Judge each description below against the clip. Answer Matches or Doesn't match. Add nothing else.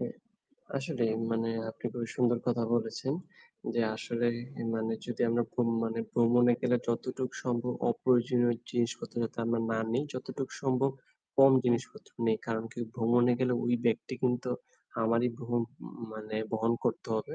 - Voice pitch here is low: Matches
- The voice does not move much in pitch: Matches